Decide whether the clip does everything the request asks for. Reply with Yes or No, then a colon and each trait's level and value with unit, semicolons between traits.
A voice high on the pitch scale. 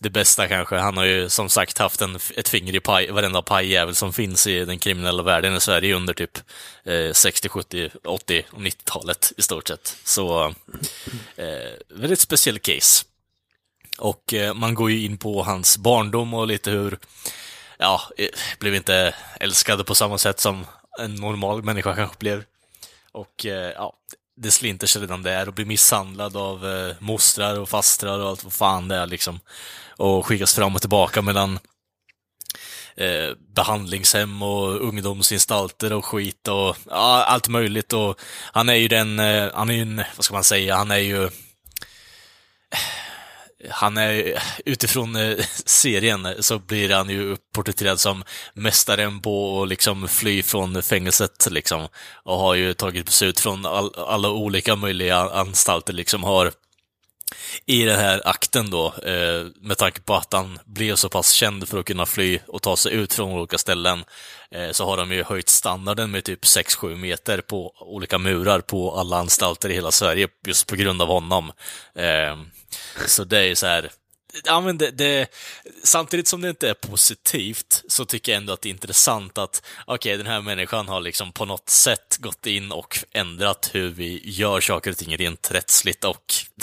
No: low, 100 Hz